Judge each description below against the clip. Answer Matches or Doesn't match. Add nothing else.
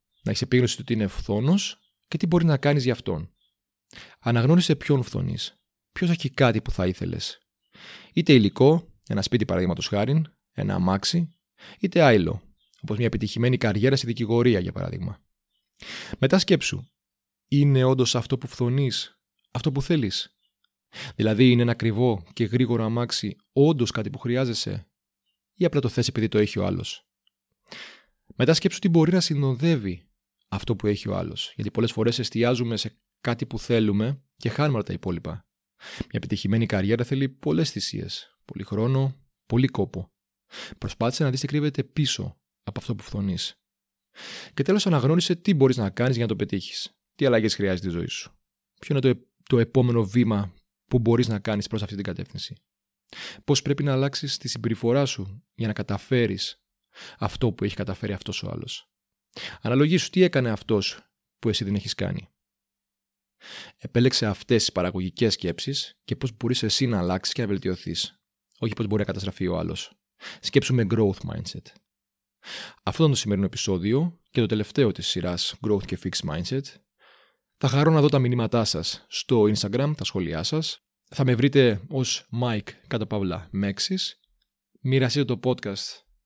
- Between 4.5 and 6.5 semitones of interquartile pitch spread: Matches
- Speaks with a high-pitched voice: Doesn't match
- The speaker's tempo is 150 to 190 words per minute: Matches